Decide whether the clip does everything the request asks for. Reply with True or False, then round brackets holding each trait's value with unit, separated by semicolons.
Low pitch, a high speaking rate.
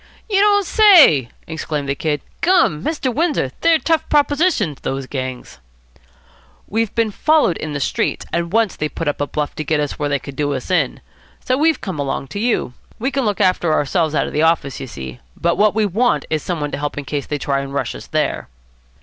False (160 Hz; 220 wpm)